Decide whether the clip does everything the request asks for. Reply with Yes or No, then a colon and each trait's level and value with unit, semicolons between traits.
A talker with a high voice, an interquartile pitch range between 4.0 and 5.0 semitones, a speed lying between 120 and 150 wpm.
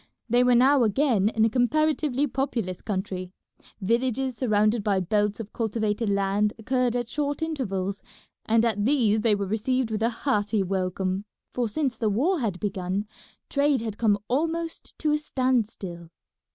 No: high, 225 Hz; average, 4.3 semitones; average, 160 wpm